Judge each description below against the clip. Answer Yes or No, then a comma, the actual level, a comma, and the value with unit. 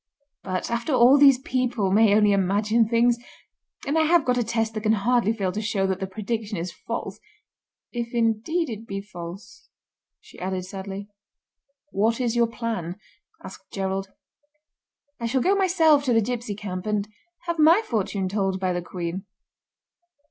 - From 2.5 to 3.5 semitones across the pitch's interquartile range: No, average, 4.0 semitones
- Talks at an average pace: Yes, average, 165 wpm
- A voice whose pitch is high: Yes, high, 220 Hz